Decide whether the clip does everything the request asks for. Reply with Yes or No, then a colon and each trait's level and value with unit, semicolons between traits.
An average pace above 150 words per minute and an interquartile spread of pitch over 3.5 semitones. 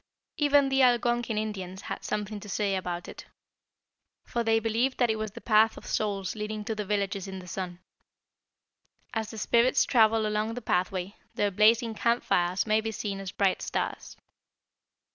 No: average, 175 wpm; narrow, 2.5 semitones